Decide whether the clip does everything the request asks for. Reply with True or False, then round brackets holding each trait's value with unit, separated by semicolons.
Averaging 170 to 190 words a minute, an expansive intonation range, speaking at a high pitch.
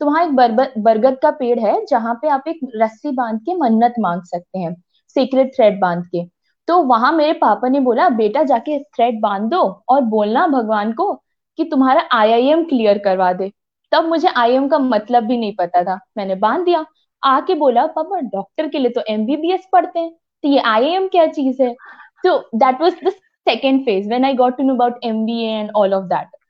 True (185 wpm; 6.1 semitones; 255 Hz)